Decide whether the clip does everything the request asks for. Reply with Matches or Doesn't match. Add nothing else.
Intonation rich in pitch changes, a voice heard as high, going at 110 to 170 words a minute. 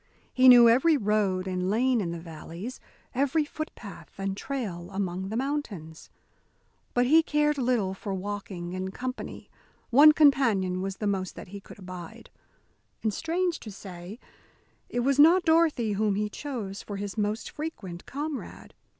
Matches